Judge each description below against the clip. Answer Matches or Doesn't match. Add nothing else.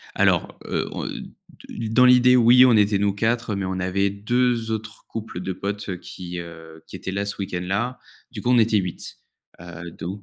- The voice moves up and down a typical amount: Matches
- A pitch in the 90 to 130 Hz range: Matches